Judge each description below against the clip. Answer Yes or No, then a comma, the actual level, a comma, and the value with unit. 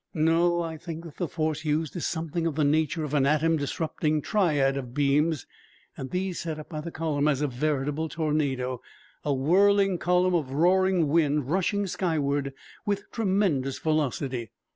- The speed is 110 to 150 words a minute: No, average, 165 wpm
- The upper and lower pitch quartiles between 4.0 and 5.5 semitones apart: No, average, 3.2 semitones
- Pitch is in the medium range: Yes, medium, 155 Hz